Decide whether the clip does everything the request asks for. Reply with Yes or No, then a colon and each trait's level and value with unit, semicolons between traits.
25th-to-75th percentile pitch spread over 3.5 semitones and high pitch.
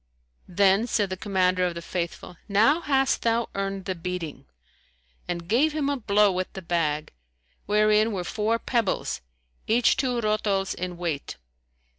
Yes: average, 3.9 semitones; high, 200 Hz